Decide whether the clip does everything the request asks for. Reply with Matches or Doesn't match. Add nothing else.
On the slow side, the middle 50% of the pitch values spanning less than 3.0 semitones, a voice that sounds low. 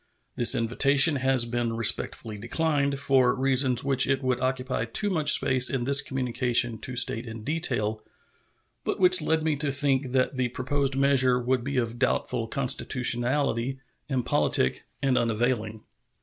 Doesn't match